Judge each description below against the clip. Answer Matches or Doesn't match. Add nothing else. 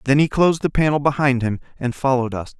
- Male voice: Matches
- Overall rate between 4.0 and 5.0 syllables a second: Doesn't match